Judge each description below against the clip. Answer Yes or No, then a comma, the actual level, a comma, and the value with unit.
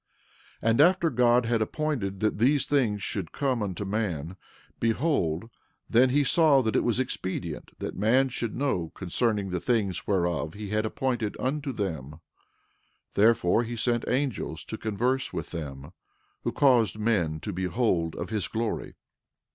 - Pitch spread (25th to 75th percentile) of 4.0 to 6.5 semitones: Yes, average, 5.0 semitones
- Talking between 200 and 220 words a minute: No, average, 155 wpm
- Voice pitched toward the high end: No, low, 110 Hz